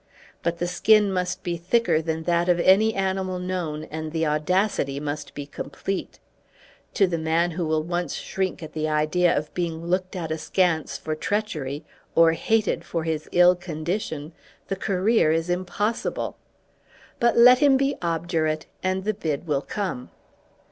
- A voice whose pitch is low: No, medium, 175 Hz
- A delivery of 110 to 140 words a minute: No, average, 160 wpm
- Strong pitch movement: No, average, 3.1 semitones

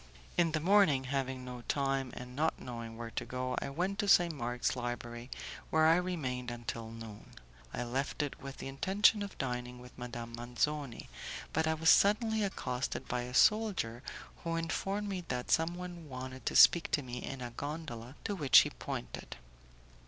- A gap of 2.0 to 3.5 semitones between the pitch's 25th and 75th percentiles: No, average, 5.2 semitones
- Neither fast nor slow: Yes, average, 175 wpm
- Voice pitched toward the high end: No, low, 135 Hz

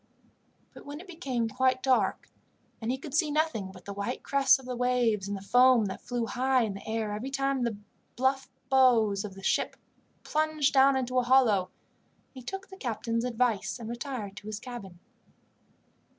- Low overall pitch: No, very high, 250 Hz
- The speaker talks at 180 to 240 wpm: Yes, average, 185 wpm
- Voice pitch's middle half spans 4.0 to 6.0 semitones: No, average, 3.5 semitones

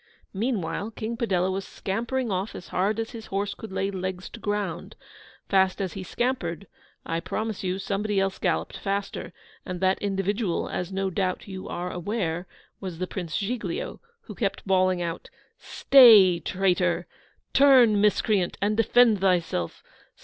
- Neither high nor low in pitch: No, high, 195 Hz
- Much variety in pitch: No, average, 2.8 semitones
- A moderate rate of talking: Yes, average, 150 wpm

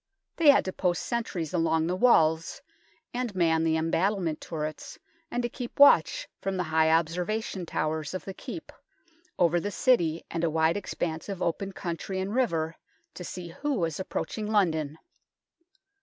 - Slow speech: No, average, 165 wpm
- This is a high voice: No, medium, 175 Hz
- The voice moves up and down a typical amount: Yes, average, 4.1 semitones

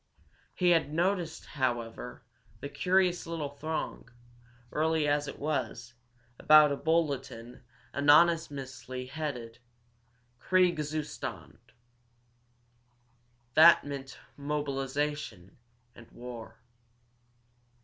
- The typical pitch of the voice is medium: Yes, medium, 145 Hz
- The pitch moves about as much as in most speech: Yes, average, 3.7 semitones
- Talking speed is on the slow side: Yes, slow, 75 wpm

